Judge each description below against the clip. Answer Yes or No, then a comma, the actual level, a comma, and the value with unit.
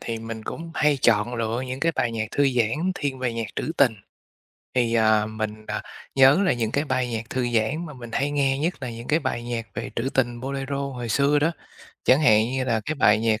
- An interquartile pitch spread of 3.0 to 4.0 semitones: Yes, average, 3.6 semitones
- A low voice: Yes, low, 125 Hz